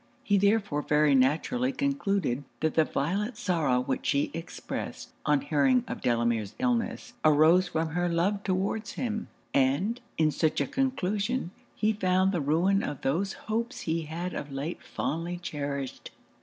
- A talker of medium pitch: Yes, medium, 170 Hz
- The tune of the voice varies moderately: No, wide, 5.8 semitones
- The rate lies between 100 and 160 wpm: Yes, average, 150 wpm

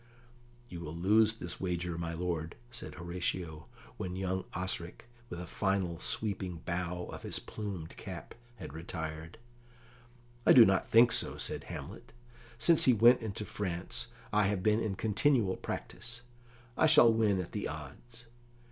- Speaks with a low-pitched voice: Yes, very low, 95 Hz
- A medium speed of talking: Yes, average, 150 wpm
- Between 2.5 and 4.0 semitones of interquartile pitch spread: No, average, 4.4 semitones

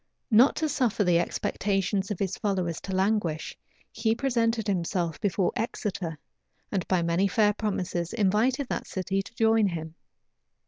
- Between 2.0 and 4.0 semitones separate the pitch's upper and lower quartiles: Yes, average, 3.7 semitones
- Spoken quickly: No, average, 145 wpm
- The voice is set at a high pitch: Yes, high, 195 Hz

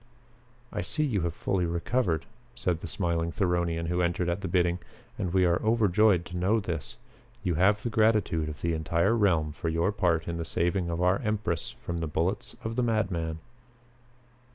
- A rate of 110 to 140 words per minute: No, average, 185 wpm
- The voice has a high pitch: No, very low, 90 Hz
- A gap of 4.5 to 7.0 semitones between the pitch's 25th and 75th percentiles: No, average, 3.4 semitones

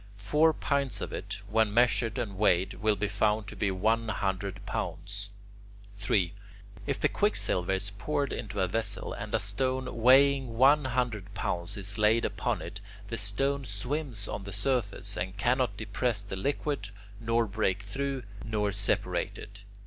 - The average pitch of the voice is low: Yes, low, 105 Hz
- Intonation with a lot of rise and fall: No, average, 3.8 semitones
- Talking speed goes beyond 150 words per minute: Yes, average, 160 wpm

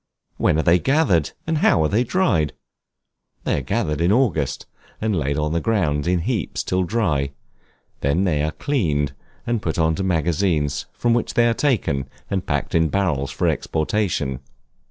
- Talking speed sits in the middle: Yes, average, 170 wpm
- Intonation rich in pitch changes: Yes, wide, 6.4 semitones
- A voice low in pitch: Yes, very low, 85 Hz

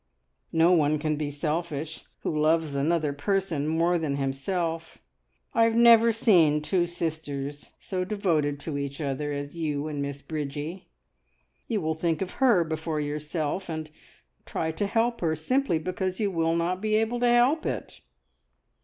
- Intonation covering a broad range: No, average, 4.0 semitones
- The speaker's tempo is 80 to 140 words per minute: No, average, 160 wpm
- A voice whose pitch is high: No, medium, 160 Hz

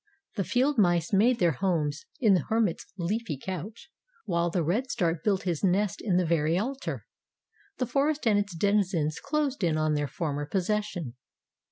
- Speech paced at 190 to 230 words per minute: No, average, 170 wpm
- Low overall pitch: No, medium, 185 Hz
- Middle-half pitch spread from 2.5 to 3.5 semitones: No, average, 4.9 semitones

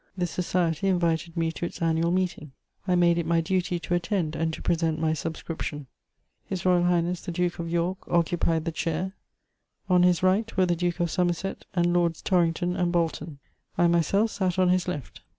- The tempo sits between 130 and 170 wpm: No, average, 185 wpm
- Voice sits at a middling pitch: Yes, medium, 175 Hz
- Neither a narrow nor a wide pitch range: No, narrow, 1.5 semitones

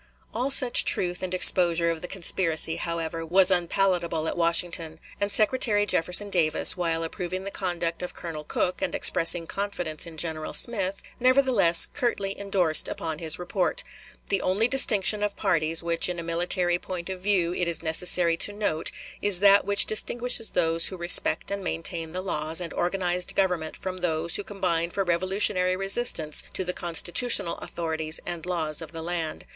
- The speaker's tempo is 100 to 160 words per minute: No, average, 170 wpm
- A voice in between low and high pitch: Yes, medium, 180 Hz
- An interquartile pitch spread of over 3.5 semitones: No, average, 2.9 semitones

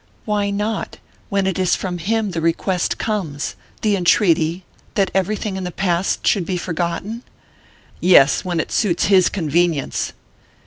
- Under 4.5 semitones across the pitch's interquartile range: Yes, average, 2.9 semitones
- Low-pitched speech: No, medium, 185 Hz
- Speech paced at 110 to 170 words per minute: Yes, average, 145 wpm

